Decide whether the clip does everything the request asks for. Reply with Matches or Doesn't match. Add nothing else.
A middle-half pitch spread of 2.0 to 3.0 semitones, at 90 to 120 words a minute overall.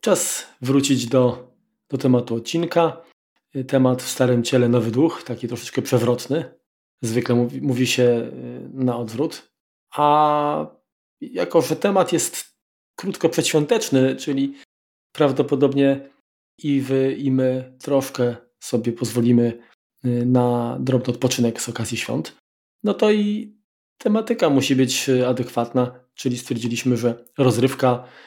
Matches